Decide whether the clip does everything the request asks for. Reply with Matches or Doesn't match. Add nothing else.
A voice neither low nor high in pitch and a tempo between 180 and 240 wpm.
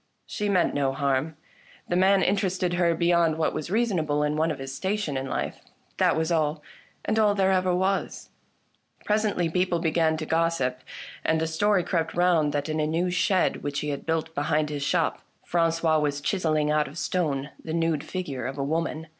Matches